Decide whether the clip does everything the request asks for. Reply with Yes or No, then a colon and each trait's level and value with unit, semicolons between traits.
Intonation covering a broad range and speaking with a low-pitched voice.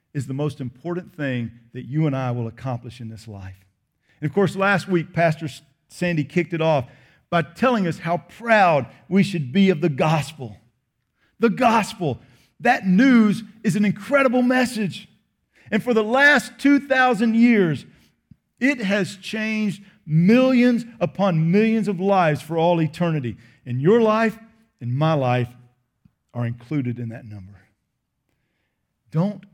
No: wide, 8.5 semitones; medium, 170 Hz